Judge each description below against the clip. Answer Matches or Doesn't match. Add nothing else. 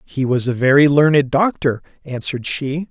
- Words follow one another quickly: Doesn't match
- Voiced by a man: Matches